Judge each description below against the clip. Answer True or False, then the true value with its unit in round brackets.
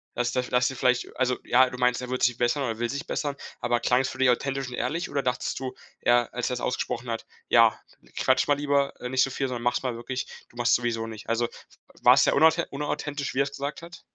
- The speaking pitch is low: True (125 Hz)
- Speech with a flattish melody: True (2.2 semitones)